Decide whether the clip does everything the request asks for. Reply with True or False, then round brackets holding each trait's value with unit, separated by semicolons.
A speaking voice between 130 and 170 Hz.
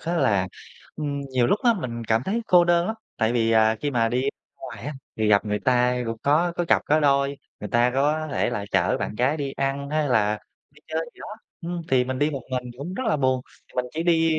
True (135 Hz)